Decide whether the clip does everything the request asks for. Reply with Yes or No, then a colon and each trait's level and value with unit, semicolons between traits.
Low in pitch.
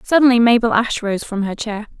No: high, 225 Hz